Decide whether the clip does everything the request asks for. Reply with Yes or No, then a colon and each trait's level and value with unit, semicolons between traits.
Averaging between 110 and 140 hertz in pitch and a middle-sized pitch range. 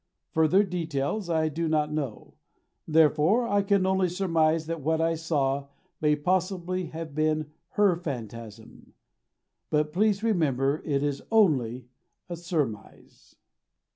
No: medium, 160 Hz; average, 3.7 semitones